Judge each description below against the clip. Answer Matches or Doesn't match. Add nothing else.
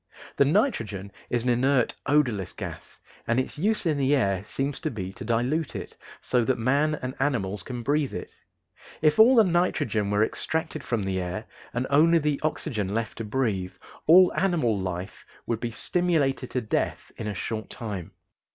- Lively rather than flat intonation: Matches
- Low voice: Matches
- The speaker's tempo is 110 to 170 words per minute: Doesn't match